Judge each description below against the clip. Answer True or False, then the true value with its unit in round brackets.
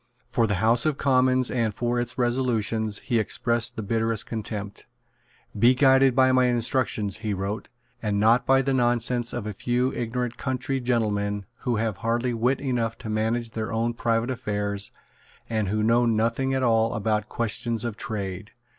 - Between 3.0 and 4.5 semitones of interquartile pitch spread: False (2.4 semitones)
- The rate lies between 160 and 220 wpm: True (170 wpm)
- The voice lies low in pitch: True (115 Hz)